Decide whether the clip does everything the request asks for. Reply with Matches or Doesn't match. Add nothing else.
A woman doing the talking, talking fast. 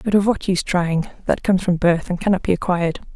Matches